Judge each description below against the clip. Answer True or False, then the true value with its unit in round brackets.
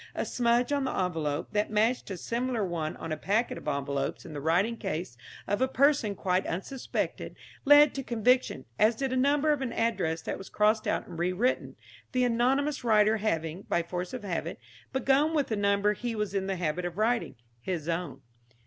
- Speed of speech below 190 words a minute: False (195 wpm)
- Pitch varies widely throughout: True (6.1 semitones)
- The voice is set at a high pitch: True (210 Hz)